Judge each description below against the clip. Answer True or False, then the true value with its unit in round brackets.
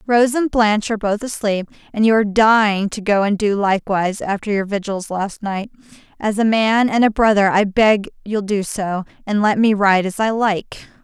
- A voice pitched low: False (210 Hz)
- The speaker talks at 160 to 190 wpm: False (205 wpm)